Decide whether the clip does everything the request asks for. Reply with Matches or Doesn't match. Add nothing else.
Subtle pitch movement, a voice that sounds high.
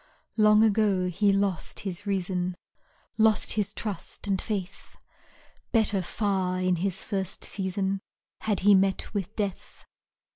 Matches